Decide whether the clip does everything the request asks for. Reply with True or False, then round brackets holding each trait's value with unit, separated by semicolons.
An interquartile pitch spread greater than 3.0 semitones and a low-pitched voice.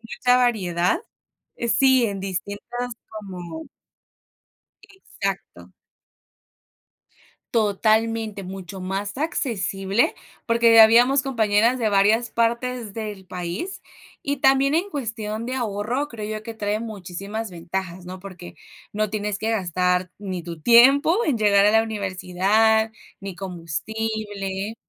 False (3.4 semitones; 215 Hz)